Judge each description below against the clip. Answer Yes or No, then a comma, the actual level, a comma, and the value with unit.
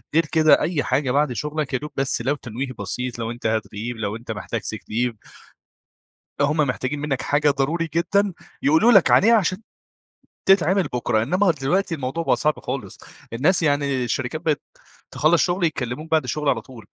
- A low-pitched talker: No, medium, 145 Hz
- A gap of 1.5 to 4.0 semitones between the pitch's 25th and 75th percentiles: No, average, 4.6 semitones